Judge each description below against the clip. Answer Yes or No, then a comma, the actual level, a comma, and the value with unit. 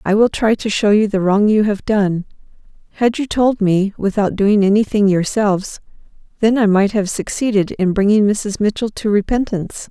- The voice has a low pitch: No, high, 205 Hz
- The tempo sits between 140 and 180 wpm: Yes, average, 175 wpm